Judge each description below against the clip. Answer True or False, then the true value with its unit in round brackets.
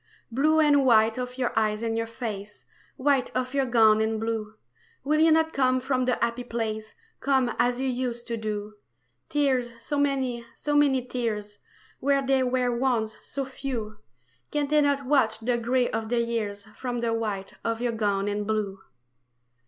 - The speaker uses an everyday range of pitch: True (3.2 semitones)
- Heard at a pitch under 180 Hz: False (240 Hz)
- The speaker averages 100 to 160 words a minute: False (175 wpm)